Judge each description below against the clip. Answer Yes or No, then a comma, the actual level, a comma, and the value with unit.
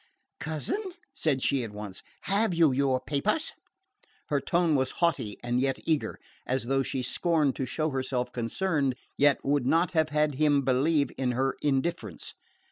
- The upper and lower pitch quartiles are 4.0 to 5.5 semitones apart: No, average, 3.5 semitones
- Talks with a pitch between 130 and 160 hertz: Yes, medium, 140 Hz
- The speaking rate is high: No, average, 160 wpm